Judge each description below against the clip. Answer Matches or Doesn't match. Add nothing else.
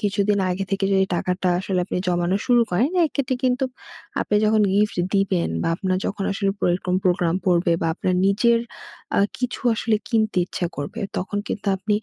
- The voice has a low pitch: Doesn't match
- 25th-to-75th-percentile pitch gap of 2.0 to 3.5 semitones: Matches